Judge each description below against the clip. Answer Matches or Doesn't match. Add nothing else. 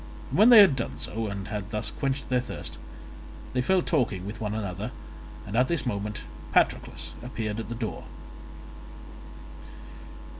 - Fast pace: Doesn't match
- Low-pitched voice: Matches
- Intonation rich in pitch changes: Doesn't match